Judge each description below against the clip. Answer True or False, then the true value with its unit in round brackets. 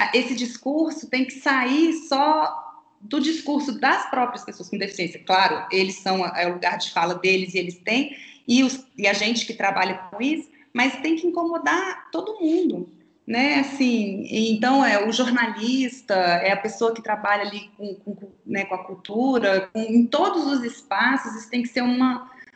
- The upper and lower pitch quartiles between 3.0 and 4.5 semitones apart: False (5.5 semitones)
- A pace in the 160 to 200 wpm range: True (185 wpm)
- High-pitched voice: True (240 Hz)